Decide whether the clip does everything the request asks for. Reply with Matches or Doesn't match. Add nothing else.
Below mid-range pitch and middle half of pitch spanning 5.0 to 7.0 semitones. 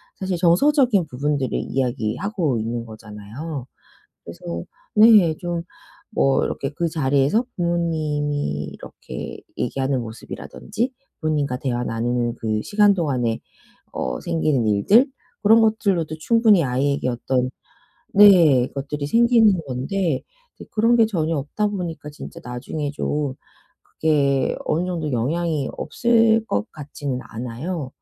Doesn't match